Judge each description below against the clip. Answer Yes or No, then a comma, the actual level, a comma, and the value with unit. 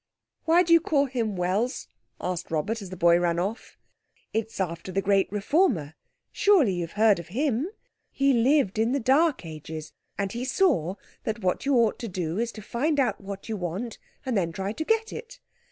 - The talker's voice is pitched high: Yes, high, 220 Hz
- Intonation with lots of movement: Yes, wide, 7.0 semitones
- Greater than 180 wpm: Yes, average, 190 wpm